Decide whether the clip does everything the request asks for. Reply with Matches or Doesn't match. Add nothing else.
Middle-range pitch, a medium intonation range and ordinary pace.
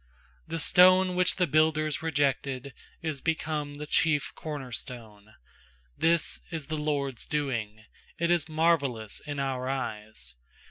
Doesn't match